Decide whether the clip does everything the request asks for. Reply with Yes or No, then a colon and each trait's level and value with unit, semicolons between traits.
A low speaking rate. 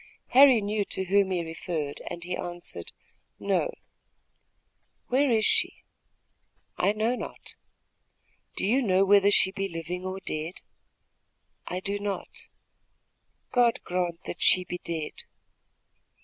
Yes: slow, 125 wpm